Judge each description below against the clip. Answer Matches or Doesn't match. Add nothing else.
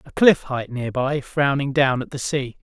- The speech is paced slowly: Doesn't match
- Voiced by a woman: Doesn't match